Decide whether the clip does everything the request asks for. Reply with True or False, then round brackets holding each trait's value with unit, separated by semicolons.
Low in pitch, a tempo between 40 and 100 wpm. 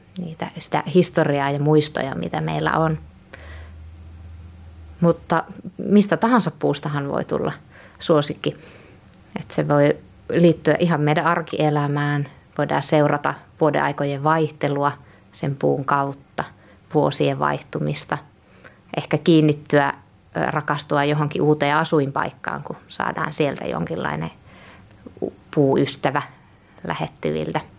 False (145 Hz; 95 wpm)